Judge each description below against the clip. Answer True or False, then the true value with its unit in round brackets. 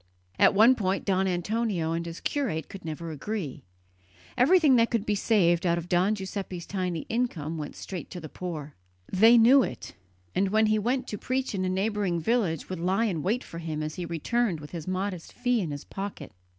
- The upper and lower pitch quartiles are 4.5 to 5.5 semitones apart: True (4.8 semitones)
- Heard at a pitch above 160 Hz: True (190 Hz)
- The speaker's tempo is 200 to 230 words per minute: True (205 wpm)